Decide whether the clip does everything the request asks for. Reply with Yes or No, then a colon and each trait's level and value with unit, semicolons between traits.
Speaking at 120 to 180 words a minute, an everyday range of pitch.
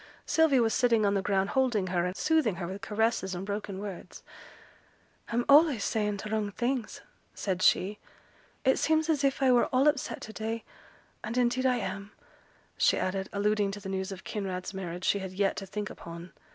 No: average, 190 wpm; average, 4.2 semitones